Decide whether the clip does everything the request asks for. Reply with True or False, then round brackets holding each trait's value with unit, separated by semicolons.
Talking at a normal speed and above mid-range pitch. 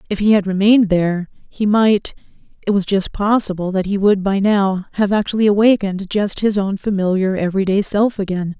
True (190 wpm; 200 Hz)